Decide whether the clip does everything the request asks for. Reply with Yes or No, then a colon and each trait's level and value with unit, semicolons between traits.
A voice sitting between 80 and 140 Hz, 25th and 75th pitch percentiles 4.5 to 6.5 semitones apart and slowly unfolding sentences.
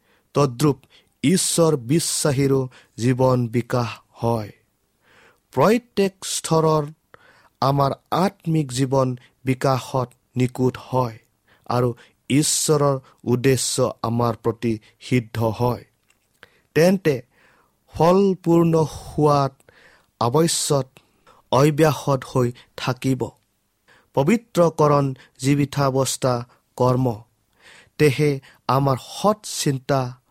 No: low, 135 Hz; average, 3.7 semitones; slow, 70 wpm